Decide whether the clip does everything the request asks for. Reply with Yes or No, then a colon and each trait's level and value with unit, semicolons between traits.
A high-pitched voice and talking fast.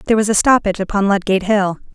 Yes: high, 200 Hz; fast, 215 wpm